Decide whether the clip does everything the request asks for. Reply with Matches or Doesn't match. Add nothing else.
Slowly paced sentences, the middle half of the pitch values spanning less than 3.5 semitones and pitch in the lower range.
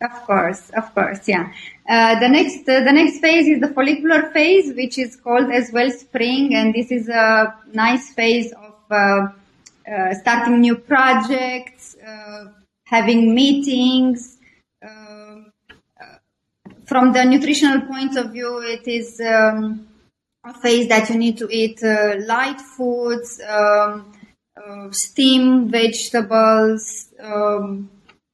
Doesn't match